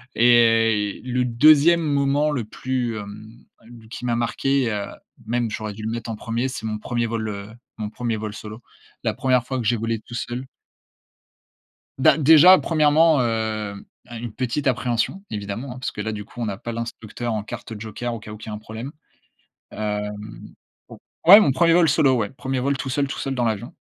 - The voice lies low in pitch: Yes, low, 120 Hz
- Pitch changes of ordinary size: Yes, average, 3.4 semitones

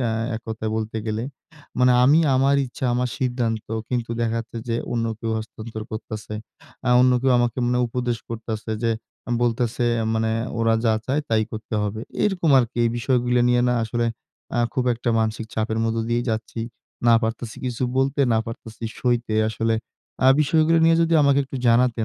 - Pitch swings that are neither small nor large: No, narrow, 2.0 semitones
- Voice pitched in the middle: No, low, 120 Hz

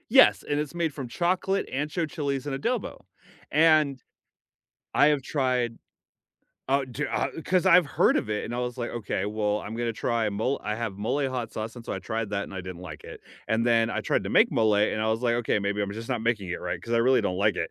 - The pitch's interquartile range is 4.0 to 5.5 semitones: Yes, average, 4.9 semitones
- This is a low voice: Yes, low, 120 Hz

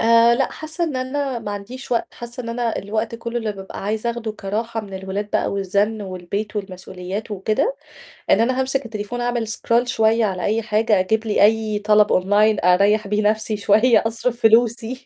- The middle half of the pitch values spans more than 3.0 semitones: No, narrow, 2.4 semitones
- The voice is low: No, high, 220 Hz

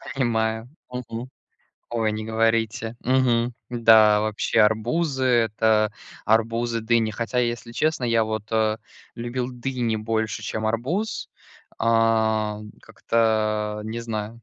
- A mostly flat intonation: Yes, narrow, 1.5 semitones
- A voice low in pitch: Yes, low, 115 Hz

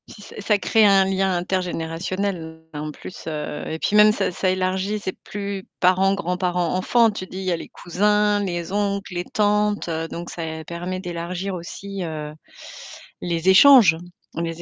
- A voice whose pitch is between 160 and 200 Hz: Yes, medium, 185 Hz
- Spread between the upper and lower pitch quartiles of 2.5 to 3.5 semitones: Yes, average, 2.8 semitones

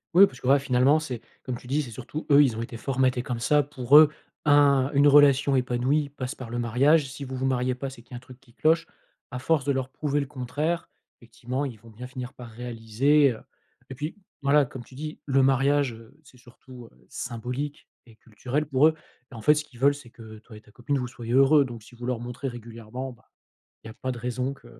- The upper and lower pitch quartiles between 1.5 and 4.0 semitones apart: Yes, average, 2.8 semitones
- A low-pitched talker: Yes, low, 130 Hz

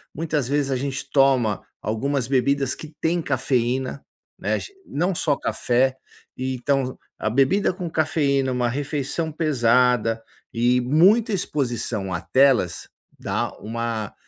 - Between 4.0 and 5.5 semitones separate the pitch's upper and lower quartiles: No, average, 3.3 semitones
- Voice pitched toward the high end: No, low, 135 Hz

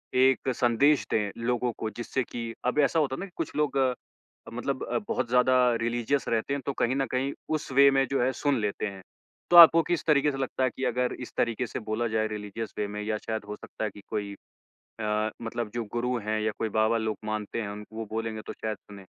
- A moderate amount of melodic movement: Yes, average, 3.5 semitones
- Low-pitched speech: Yes, low, 115 Hz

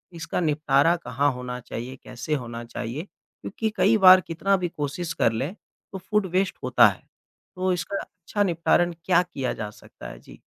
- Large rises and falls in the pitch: Yes, wide, 6.5 semitones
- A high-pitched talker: No, medium, 160 Hz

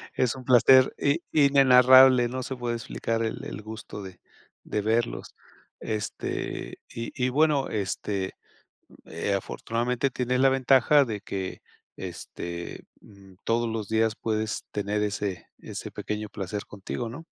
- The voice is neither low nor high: No, low, 115 Hz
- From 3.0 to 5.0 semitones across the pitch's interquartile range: Yes, average, 3.8 semitones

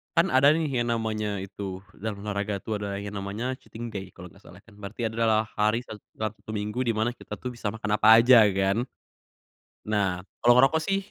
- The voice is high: No, low, 110 Hz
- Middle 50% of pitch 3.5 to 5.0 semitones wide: No, average, 2.8 semitones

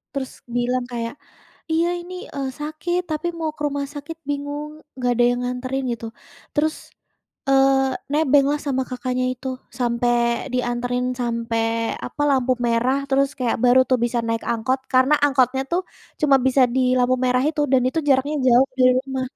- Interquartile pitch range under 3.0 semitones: Yes, narrow, 2.5 semitones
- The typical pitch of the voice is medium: No, very high, 260 Hz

